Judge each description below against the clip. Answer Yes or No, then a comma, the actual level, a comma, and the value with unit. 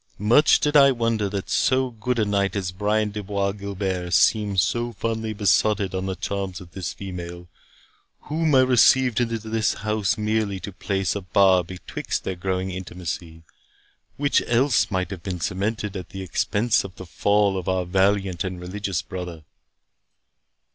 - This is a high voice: No, low, 100 Hz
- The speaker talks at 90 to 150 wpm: No, average, 165 wpm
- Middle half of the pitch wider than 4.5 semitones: No, average, 3.0 semitones